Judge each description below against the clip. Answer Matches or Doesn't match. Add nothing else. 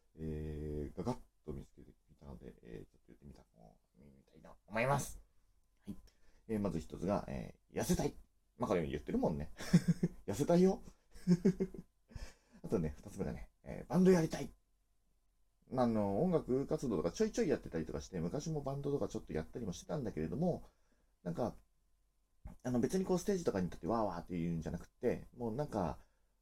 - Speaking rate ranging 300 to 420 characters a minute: Matches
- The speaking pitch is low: Matches